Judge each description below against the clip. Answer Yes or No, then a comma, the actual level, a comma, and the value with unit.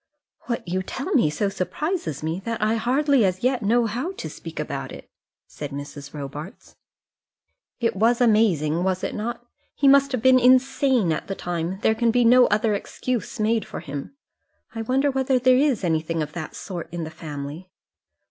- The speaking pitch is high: Yes, high, 215 Hz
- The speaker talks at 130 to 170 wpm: No, average, 185 wpm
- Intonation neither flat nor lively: No, wide, 7.1 semitones